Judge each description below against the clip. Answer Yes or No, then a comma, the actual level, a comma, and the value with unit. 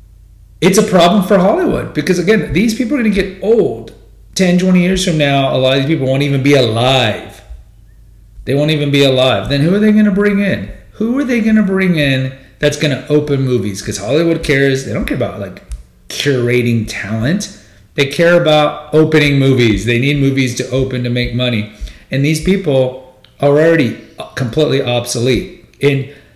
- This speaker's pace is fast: No, average, 190 wpm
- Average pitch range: No, wide, 5.7 semitones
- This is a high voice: No, medium, 140 Hz